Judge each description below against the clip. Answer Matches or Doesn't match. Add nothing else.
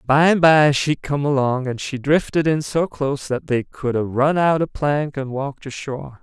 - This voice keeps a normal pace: Doesn't match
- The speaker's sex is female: Doesn't match